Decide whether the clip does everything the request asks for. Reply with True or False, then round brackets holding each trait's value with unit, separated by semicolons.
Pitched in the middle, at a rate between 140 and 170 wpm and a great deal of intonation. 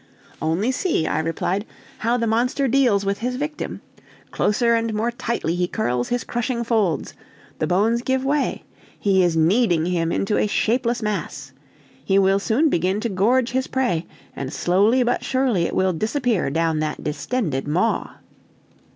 False (210 Hz; 160 wpm; 5.8 semitones)